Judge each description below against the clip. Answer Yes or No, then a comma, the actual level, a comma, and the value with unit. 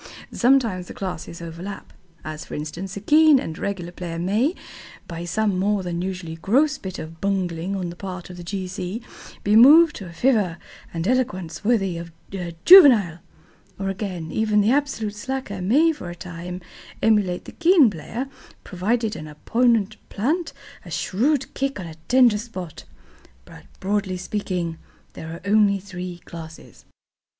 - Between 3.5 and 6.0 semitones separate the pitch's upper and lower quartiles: Yes, average, 4.7 semitones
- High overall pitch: Yes, high, 195 Hz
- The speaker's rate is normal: Yes, average, 160 wpm